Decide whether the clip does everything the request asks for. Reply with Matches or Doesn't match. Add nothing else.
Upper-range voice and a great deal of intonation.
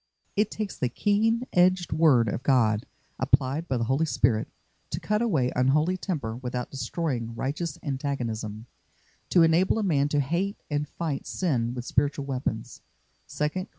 Doesn't match